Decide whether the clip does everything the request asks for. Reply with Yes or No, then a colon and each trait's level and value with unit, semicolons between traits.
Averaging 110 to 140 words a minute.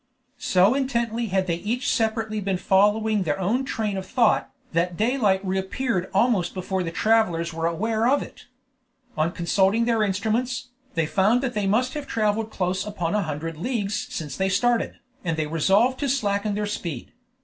No: average, 170 wpm